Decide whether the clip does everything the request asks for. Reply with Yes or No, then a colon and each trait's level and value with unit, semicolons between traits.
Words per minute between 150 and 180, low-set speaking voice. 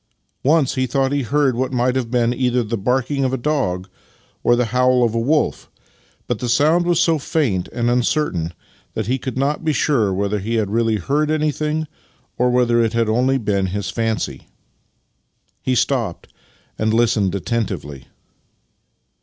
Yes: average, 170 wpm; low, 125 Hz